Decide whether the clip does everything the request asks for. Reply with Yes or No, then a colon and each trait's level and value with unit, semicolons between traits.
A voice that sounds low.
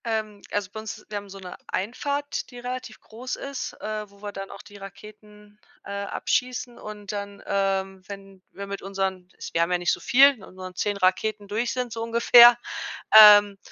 No: high, 205 Hz